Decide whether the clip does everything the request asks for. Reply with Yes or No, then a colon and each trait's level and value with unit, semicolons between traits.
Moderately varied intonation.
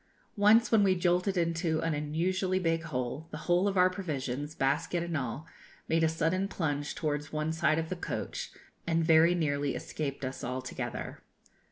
Yes: average, 3.5 semitones